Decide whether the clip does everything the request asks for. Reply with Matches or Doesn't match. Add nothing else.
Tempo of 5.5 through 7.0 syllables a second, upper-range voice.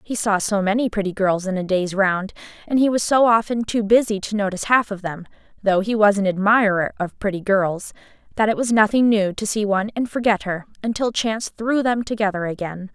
Matches